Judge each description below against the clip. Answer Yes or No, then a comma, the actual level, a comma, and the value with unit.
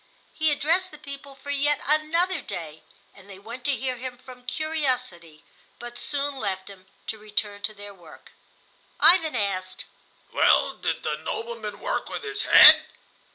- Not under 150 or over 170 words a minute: Yes, average, 155 wpm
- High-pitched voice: Yes, very high, 255 Hz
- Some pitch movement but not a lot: No, wide, 6.9 semitones